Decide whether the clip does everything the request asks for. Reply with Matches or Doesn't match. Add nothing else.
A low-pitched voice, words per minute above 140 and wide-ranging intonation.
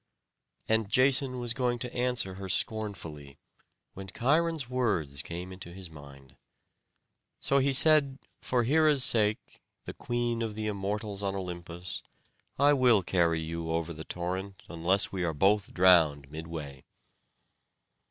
Doesn't match